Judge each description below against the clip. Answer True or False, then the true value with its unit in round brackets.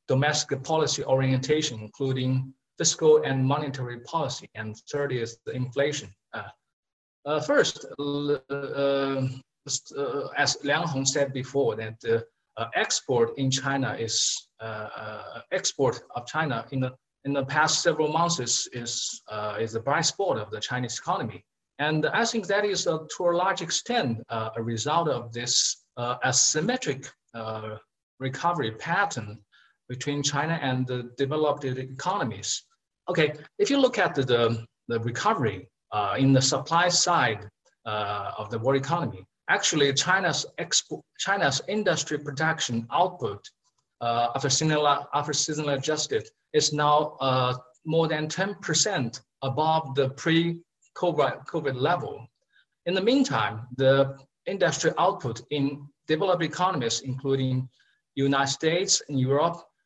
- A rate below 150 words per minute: True (135 wpm)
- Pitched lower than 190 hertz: True (140 Hz)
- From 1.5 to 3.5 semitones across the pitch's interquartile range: False (4.1 semitones)